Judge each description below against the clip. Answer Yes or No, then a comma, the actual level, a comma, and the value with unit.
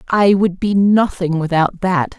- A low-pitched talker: No, medium, 185 Hz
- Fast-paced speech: No, average, 165 wpm